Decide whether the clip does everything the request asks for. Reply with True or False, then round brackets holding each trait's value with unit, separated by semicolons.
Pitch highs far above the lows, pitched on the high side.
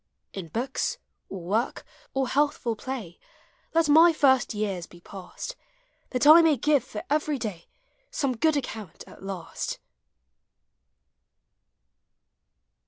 True (7.0 semitones; 255 Hz)